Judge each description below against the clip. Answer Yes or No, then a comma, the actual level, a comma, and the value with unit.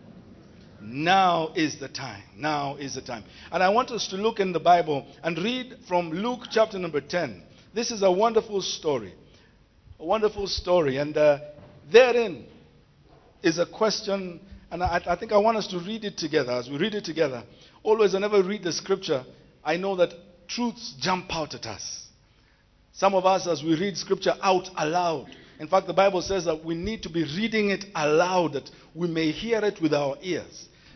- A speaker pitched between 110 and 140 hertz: No, medium, 175 Hz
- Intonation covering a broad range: No, average, 4.6 semitones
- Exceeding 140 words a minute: Yes, average, 190 wpm